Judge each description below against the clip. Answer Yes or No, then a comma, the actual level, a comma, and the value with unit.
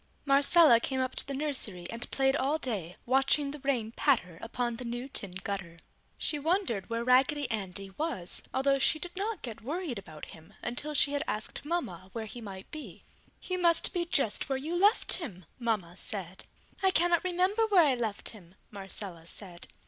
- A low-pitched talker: No, very high, 255 Hz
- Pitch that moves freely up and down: Yes, wide, 7.1 semitones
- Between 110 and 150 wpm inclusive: No, average, 185 wpm